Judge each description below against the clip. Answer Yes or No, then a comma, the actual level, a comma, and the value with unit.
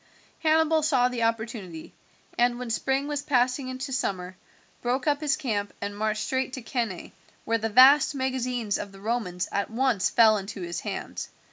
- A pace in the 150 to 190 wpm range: Yes, average, 170 wpm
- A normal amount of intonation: Yes, average, 3.9 semitones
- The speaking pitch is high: Yes, high, 240 Hz